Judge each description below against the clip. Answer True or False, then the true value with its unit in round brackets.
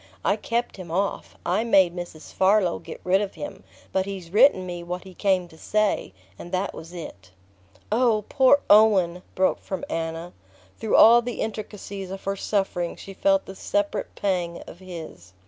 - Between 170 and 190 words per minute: True (175 wpm)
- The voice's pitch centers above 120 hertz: True (190 Hz)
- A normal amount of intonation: True (3.0 semitones)